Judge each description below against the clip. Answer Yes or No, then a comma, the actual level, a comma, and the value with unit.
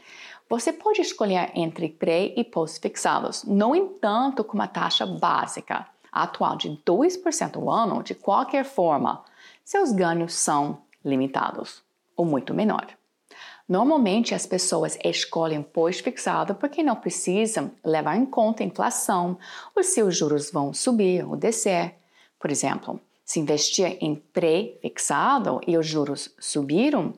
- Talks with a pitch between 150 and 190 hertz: Yes, medium, 185 Hz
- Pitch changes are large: Yes, wide, 7.5 semitones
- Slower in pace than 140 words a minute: Yes, average, 130 wpm